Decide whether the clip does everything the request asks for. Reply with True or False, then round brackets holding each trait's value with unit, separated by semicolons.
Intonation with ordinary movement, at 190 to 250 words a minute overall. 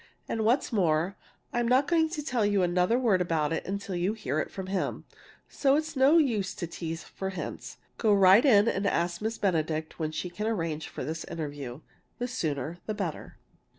False (5.7 semitones; 195 wpm)